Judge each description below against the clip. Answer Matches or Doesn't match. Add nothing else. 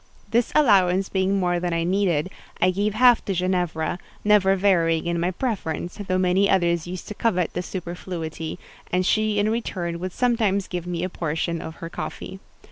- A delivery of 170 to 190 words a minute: Matches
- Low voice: Doesn't match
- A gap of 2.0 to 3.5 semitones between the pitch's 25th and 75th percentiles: Matches